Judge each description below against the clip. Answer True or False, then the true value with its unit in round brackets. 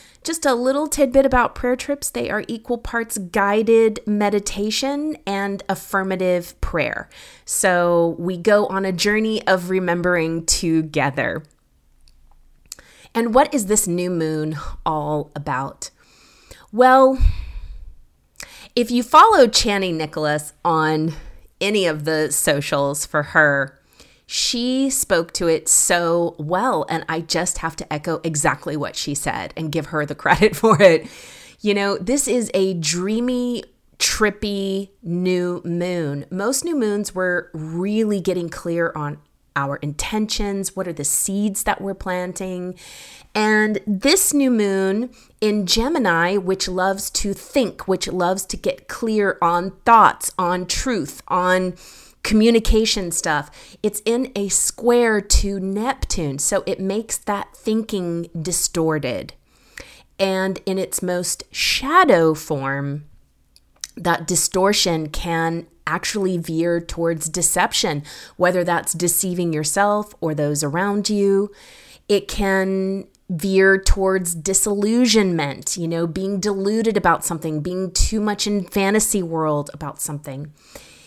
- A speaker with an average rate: False (125 wpm)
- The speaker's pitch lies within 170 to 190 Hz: True (185 Hz)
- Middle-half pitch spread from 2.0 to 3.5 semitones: False (4.3 semitones)